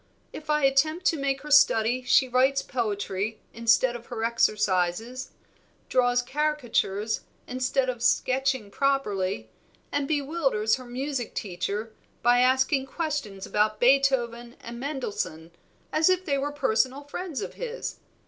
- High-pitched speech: Yes, very high, 255 Hz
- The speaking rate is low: Yes, slow, 130 wpm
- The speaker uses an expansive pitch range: No, average, 3.9 semitones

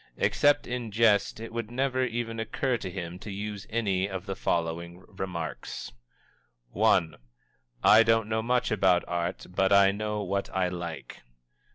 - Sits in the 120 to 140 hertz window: No, low, 100 Hz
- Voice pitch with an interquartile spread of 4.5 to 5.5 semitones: No, average, 3.9 semitones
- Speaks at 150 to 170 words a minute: Yes, average, 155 wpm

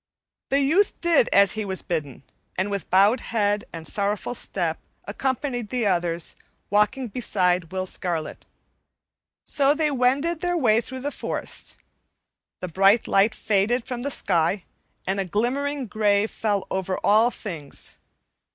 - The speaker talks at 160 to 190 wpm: No, average, 140 wpm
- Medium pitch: No, high, 210 Hz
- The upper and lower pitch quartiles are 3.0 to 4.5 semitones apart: No, average, 5.1 semitones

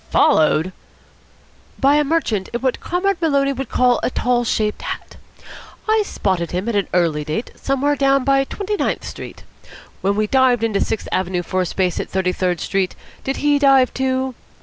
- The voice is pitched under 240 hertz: No, high, 245 Hz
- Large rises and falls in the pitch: Yes, wide, 6.5 semitones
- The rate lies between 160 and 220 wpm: Yes, average, 180 wpm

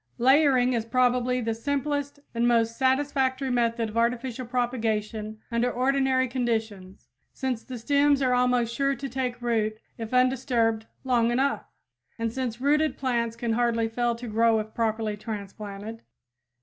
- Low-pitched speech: No, high, 240 Hz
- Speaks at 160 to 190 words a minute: No, average, 145 wpm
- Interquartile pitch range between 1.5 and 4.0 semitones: Yes, narrow, 2.4 semitones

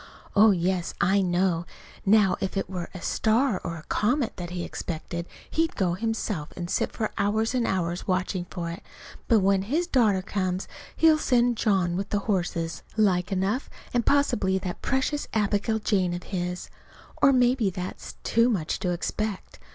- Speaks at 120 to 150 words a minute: No, average, 175 wpm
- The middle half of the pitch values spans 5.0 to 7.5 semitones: No, average, 3.8 semitones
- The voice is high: Yes, high, 195 Hz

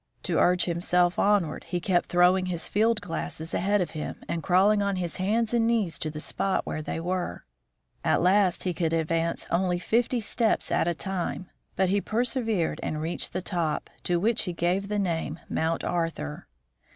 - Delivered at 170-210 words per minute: Yes, average, 185 wpm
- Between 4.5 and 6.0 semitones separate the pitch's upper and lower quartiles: No, average, 3.3 semitones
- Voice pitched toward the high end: No, medium, 180 Hz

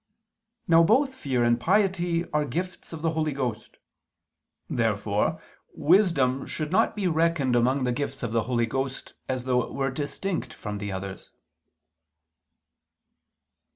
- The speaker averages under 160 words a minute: Yes, average, 140 wpm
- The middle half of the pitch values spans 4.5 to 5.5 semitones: Yes, average, 5.2 semitones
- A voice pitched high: No, medium, 140 Hz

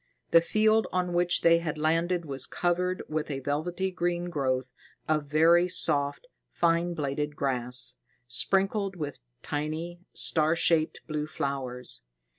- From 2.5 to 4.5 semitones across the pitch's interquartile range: Yes, average, 3.4 semitones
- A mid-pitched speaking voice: Yes, medium, 160 Hz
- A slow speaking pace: Yes, slow, 130 wpm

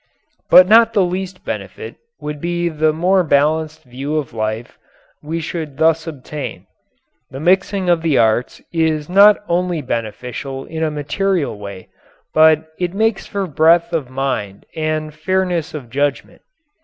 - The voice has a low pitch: No, medium, 155 Hz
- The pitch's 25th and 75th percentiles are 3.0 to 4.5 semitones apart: Yes, average, 4.0 semitones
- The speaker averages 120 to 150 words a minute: Yes, average, 145 wpm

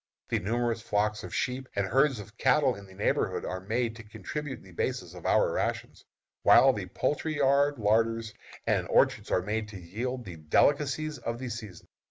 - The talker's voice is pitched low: Yes, low, 115 Hz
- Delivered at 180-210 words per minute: Yes, average, 185 wpm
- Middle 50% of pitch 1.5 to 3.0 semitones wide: No, average, 4.3 semitones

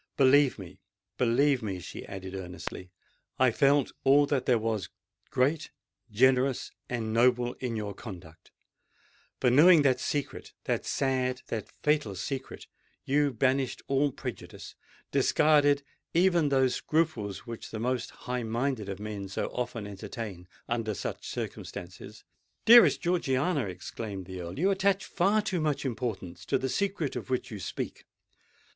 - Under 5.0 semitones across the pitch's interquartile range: No, average, 5.3 semitones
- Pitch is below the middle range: Yes, low, 125 Hz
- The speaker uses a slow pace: Yes, slow, 130 wpm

